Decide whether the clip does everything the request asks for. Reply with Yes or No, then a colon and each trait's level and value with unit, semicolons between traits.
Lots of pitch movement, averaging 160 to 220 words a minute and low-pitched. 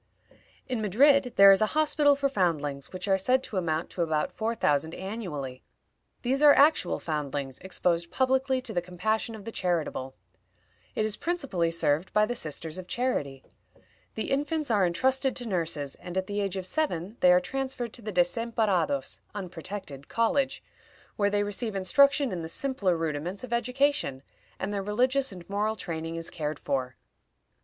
No: wide, 6.9 semitones; average, 170 wpm; high, 195 Hz